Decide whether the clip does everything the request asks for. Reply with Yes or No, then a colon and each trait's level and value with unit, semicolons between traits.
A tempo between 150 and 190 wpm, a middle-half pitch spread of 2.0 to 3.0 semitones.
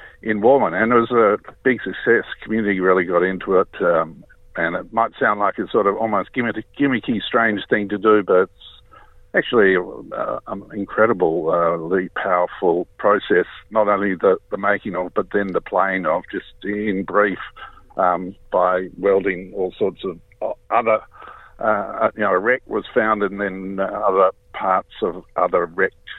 Yes: average, 165 wpm; average, 2.7 semitones